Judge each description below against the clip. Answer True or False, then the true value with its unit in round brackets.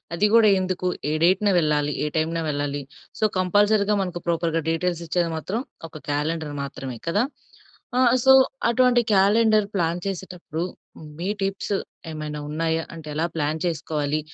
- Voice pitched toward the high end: False (170 Hz)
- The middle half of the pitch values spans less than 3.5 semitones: False (3.9 semitones)